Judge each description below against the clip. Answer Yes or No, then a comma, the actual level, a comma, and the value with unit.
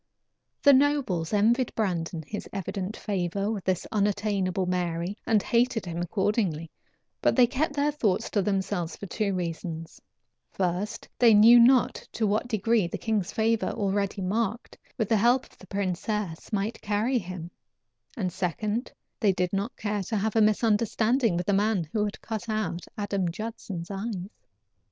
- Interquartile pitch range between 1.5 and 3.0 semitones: No, average, 3.4 semitones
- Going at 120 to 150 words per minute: No, average, 160 wpm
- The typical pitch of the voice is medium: No, high, 205 Hz